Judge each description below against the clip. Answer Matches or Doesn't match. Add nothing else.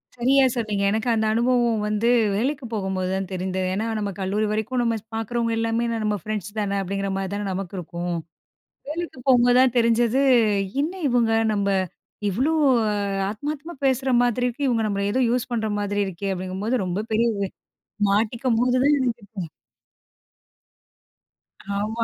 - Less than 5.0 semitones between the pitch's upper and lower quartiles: Matches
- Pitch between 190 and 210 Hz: Doesn't match